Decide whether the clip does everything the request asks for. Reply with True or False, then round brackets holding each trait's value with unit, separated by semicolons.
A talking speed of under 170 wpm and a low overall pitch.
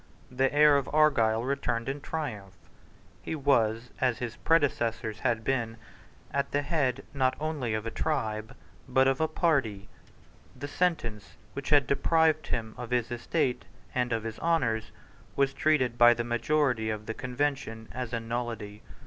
True (155 wpm; 125 Hz)